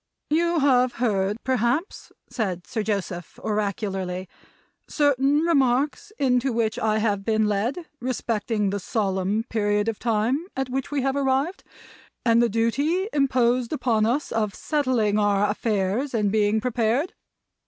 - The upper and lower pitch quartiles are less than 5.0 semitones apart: Yes, average, 4.3 semitones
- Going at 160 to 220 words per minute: No, slow, 135 wpm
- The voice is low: No, high, 230 Hz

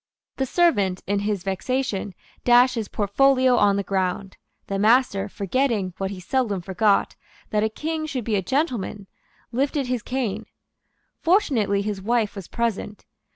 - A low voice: No, high, 215 Hz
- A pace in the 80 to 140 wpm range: No, average, 150 wpm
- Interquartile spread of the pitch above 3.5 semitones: Yes, average, 4.6 semitones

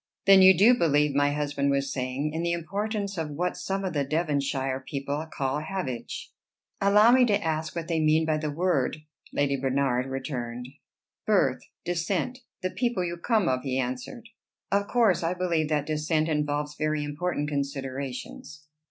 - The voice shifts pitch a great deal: No, average, 4.4 semitones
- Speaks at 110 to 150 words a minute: No, average, 165 wpm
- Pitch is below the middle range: No, medium, 155 Hz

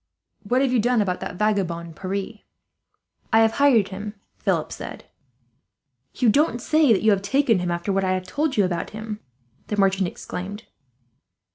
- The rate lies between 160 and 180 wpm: Yes, average, 170 wpm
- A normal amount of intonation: Yes, average, 3.5 semitones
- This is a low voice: No, high, 205 Hz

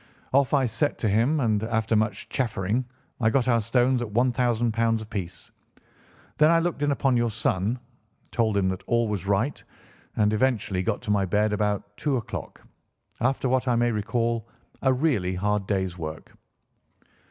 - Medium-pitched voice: No, low, 115 Hz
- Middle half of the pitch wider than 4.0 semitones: No, average, 3.4 semitones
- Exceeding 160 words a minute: Yes, average, 170 wpm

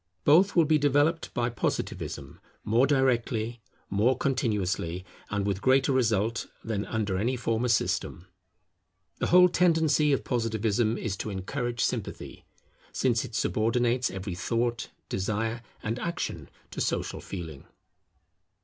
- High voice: No, low, 115 Hz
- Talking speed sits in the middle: No, slow, 125 wpm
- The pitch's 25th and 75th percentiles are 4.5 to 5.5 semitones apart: No, average, 3.9 semitones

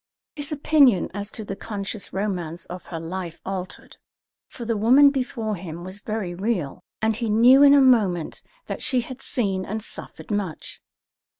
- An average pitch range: Yes, average, 4.6 semitones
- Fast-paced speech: No, average, 170 wpm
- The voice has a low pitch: No, high, 210 Hz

